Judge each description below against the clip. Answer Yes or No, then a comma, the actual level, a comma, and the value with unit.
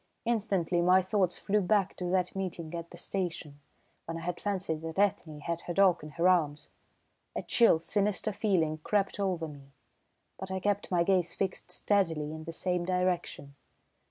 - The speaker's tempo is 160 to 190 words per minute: Yes, average, 175 wpm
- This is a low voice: No, medium, 180 Hz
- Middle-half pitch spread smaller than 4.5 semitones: Yes, average, 2.9 semitones